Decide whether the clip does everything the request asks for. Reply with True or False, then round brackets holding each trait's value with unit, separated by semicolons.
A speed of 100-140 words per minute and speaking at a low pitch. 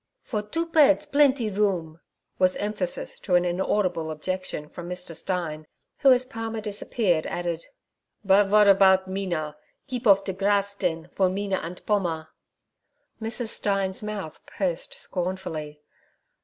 False (135 wpm; 190 Hz)